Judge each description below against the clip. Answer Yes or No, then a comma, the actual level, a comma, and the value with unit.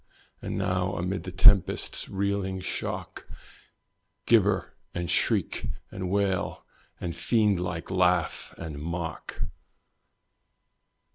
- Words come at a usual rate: No, slow, 95 wpm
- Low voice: Yes, very low, 90 Hz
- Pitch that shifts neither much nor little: No, narrow, 1.8 semitones